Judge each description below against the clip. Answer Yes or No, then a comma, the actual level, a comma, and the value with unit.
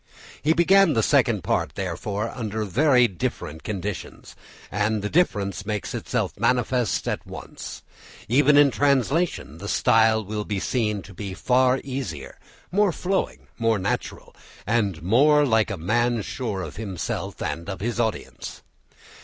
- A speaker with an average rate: Yes, average, 150 wpm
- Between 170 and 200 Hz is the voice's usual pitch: No, low, 110 Hz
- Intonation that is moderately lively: Yes, average, 4.7 semitones